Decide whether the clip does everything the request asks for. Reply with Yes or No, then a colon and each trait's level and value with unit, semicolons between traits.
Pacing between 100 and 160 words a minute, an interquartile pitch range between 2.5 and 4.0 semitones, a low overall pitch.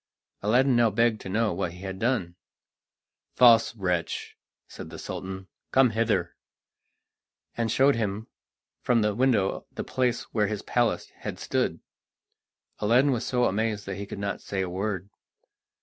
Yes: average, 150 wpm; average, 3.6 semitones; low, 110 Hz